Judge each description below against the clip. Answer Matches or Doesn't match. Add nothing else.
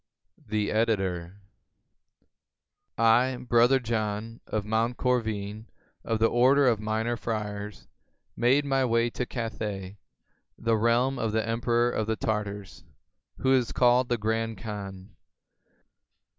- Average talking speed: Doesn't match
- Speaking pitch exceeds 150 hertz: Doesn't match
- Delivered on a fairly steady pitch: Matches